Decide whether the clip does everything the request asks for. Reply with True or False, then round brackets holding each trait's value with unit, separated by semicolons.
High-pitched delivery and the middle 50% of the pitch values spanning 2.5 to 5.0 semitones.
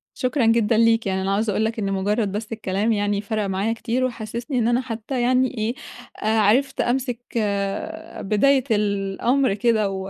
True (225 Hz; 2.9 semitones)